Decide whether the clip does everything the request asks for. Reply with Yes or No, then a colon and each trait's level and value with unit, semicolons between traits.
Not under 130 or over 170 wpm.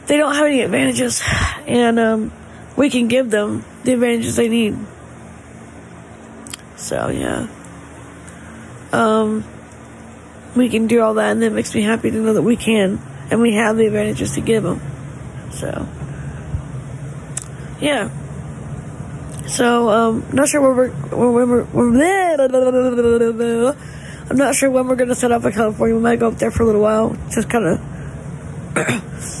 Yes: average, 145 wpm